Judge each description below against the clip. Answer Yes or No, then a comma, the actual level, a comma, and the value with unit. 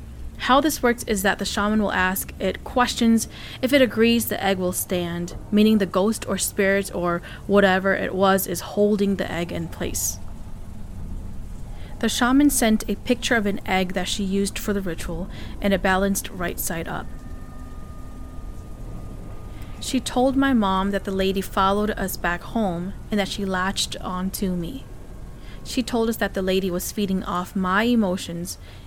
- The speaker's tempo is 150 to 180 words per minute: Yes, average, 170 wpm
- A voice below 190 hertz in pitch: No, high, 195 Hz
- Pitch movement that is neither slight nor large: Yes, average, 3.4 semitones